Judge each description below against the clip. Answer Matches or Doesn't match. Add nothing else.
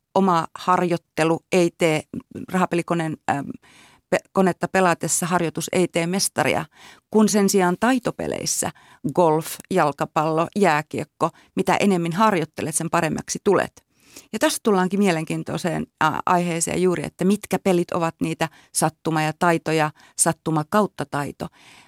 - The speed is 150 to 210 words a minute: Doesn't match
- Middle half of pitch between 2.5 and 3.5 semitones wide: Matches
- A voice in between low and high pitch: Matches